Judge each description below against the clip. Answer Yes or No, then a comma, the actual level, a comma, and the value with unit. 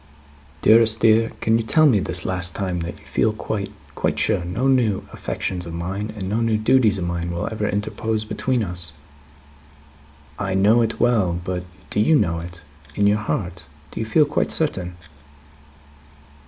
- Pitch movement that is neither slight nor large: Yes, average, 4.1 semitones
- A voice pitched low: Yes, low, 105 Hz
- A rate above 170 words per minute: Yes, average, 180 wpm